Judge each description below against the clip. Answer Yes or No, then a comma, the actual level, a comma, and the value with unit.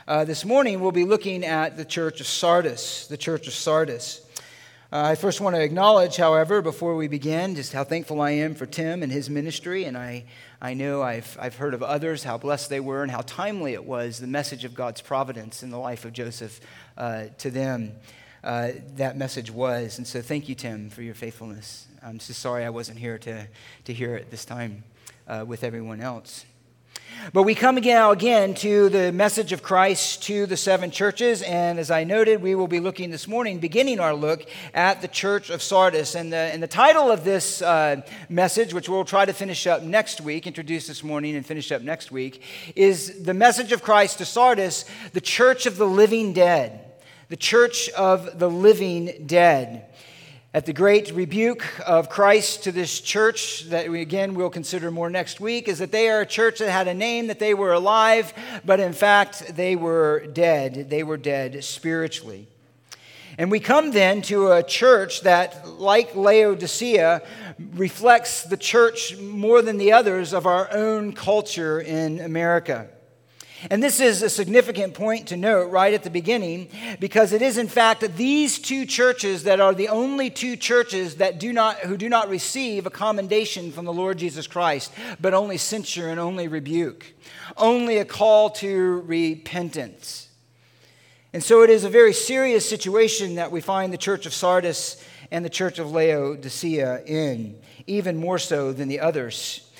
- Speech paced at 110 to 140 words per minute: No, average, 190 wpm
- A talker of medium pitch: Yes, medium, 175 Hz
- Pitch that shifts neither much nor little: No, wide, 5.9 semitones